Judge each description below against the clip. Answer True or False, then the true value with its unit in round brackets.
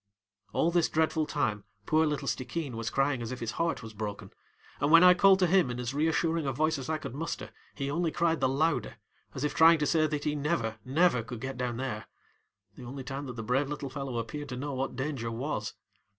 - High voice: False (140 Hz)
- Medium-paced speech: False (225 wpm)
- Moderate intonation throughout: True (4.4 semitones)